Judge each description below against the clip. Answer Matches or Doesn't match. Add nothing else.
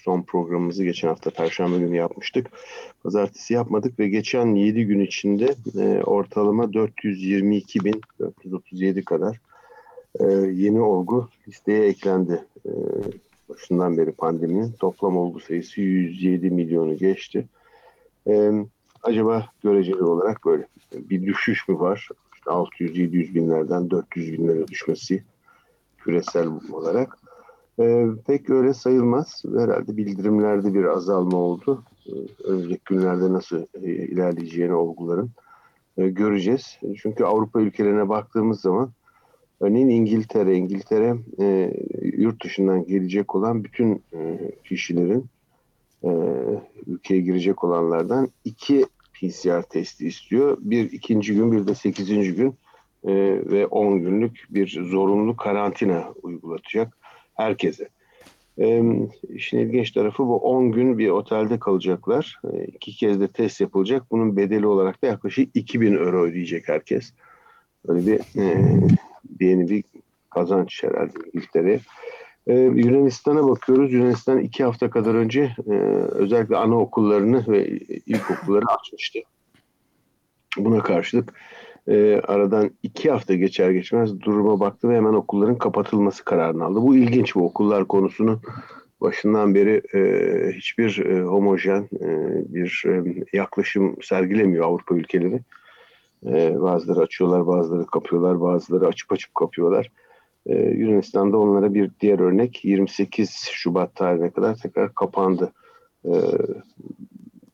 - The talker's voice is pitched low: Matches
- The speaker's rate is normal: Matches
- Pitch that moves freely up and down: Doesn't match